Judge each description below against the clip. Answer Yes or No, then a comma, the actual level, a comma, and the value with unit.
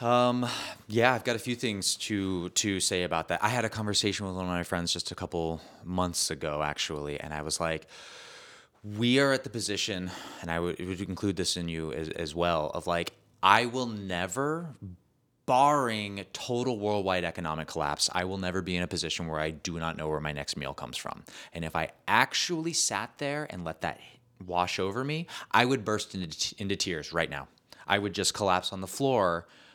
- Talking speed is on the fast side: Yes, fast, 210 wpm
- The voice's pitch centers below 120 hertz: Yes, very low, 95 Hz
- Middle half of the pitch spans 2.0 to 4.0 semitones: No, average, 5.0 semitones